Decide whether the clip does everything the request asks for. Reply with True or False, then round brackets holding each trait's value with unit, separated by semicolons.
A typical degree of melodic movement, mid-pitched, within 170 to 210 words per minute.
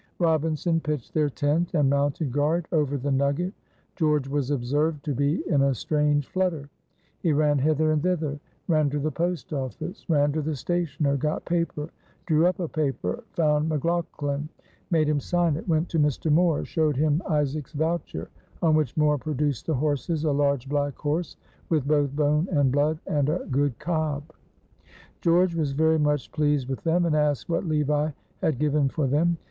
False (2.1 semitones; 150 Hz; 175 wpm)